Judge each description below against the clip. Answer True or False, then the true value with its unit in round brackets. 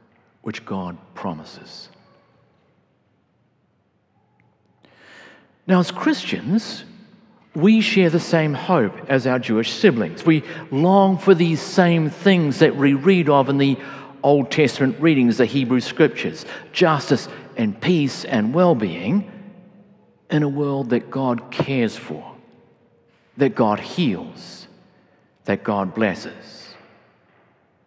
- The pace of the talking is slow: True (110 wpm)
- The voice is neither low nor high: True (160 Hz)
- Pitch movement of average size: False (6.1 semitones)